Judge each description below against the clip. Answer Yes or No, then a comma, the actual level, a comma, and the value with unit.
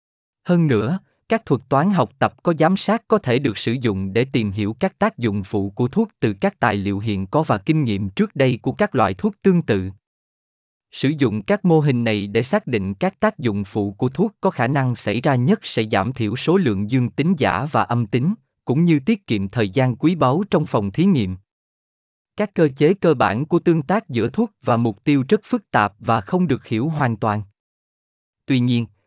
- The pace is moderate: Yes, average, 225 wpm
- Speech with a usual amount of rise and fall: No, wide, 8.6 semitones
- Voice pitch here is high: No, low, 125 Hz